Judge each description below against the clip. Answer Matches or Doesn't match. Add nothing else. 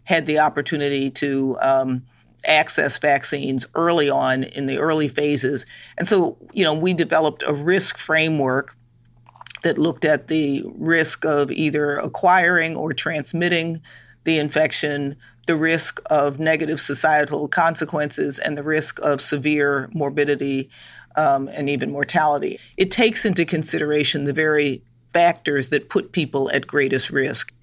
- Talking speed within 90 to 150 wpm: Matches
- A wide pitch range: Doesn't match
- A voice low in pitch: Doesn't match